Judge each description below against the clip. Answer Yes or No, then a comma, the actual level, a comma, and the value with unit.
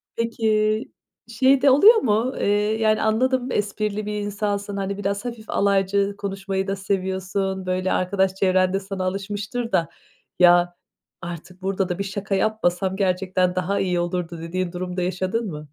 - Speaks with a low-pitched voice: No, high, 195 Hz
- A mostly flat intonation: Yes, narrow, 2.2 semitones